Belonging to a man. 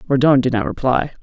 Yes: male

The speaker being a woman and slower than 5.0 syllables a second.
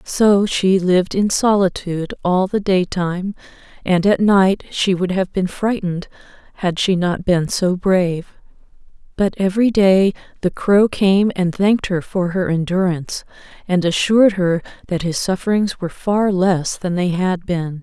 Yes: female; 4.5 syllables/s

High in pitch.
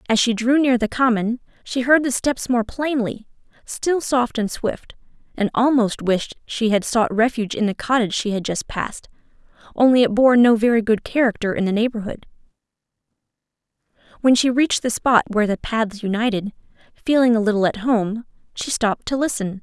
Yes: high, 230 Hz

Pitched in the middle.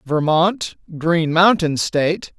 Yes: medium, 165 Hz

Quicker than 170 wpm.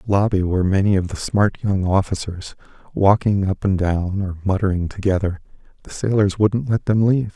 Yes: average, 190 wpm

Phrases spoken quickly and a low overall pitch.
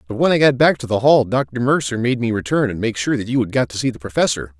Yes: fast, 315 wpm; low, 120 Hz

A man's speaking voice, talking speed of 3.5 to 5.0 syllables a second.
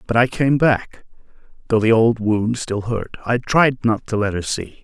Yes: male; 4.4 syllables/s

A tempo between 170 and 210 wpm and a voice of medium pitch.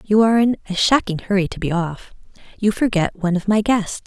No: fast, 205 wpm; high, 200 Hz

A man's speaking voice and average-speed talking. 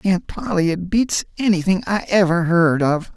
Yes: male; average, 170 wpm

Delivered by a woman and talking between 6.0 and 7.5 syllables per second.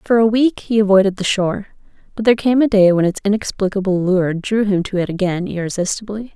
Yes: female; 6.1 syllables/s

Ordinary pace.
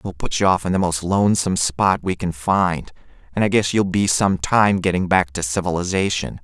No: fast, 215 wpm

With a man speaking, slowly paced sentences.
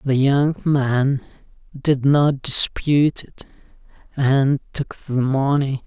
Yes: male; slow, 115 wpm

